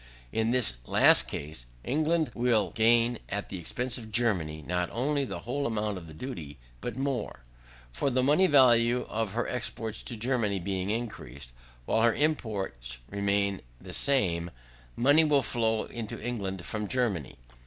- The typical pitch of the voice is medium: No, low, 110 Hz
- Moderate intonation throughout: Yes, average, 4.5 semitones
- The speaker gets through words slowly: No, average, 155 wpm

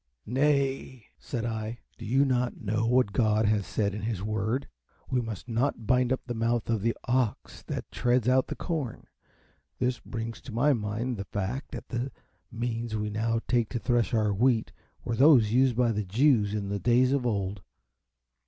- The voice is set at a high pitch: No, low, 115 Hz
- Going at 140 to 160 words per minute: No, average, 185 wpm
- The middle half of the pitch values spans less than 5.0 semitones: Yes, average, 2.8 semitones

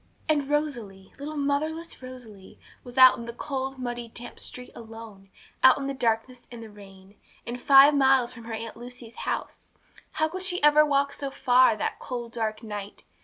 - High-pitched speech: Yes, very high, 250 Hz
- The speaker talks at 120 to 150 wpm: No, average, 180 wpm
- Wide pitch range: No, average, 3.7 semitones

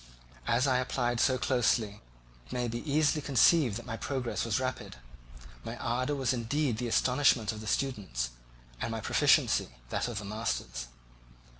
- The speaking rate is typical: Yes, average, 160 wpm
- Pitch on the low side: Yes, low, 120 Hz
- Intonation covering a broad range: No, average, 2.9 semitones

